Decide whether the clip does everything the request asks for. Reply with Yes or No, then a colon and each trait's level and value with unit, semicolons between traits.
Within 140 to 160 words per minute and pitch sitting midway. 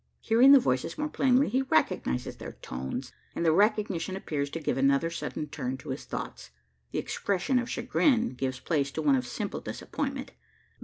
No: average, 175 wpm; medium, 165 Hz